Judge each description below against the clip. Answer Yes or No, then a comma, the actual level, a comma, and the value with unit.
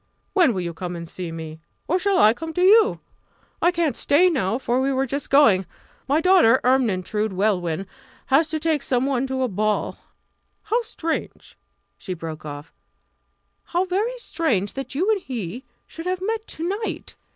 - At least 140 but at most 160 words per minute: No, average, 175 wpm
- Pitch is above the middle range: Yes, very high, 265 Hz